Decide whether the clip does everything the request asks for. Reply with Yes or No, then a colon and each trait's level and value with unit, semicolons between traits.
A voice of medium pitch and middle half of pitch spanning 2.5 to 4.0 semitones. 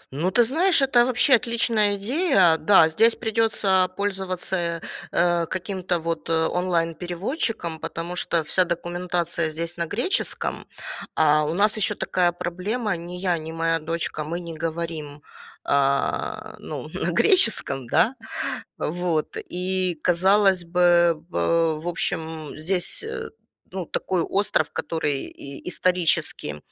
Yes: medium, 175 Hz; average, 2.9 semitones